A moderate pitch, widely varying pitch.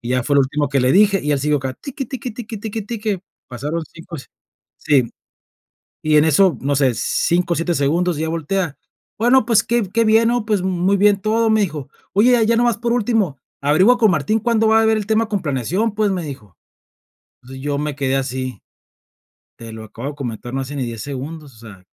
Yes: medium, 165 Hz; wide, 8.0 semitones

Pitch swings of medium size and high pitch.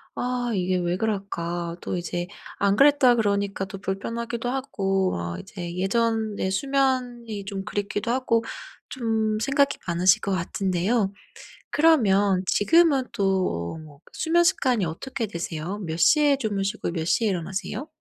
Yes: average, 4.7 semitones; high, 200 Hz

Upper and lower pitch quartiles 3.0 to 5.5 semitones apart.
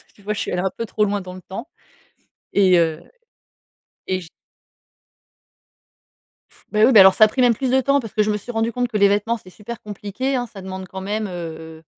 Yes: average, 3.5 semitones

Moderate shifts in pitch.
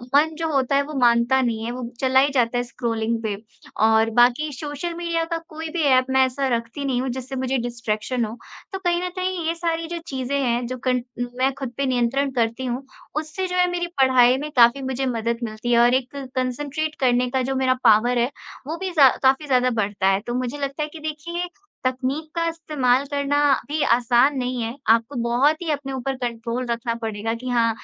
Yes: average, 3.4 semitones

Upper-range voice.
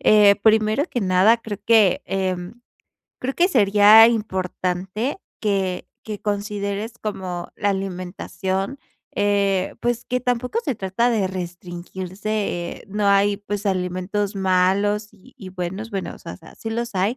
Yes: high, 200 Hz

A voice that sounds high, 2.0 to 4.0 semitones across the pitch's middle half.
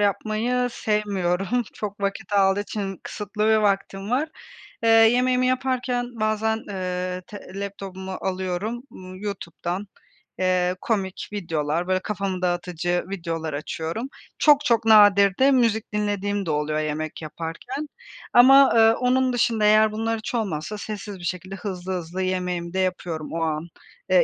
Yes: high, 200 Hz; average, 3.6 semitones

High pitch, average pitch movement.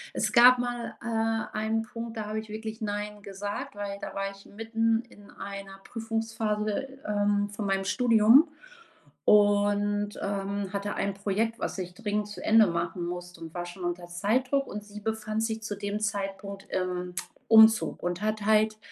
No: high, 210 Hz; narrow, 2.1 semitones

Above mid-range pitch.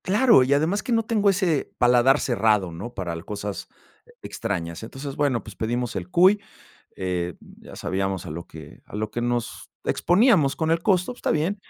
No: low, 120 Hz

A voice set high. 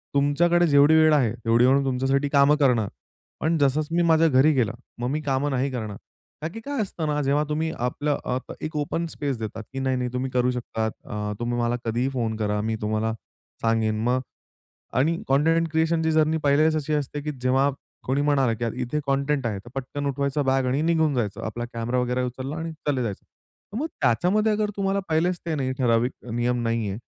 No: low, 135 Hz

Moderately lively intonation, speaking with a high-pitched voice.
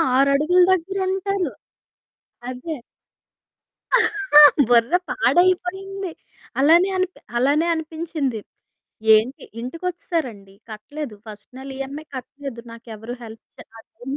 No: wide, 6.7 semitones; very high, 290 Hz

